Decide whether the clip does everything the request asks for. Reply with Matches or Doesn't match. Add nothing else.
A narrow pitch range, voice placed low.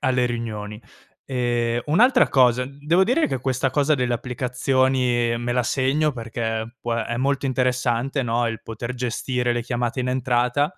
Matches